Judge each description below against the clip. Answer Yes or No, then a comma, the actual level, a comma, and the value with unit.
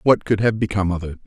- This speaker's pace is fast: Yes, fast, 285 wpm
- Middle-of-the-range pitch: No, low, 100 Hz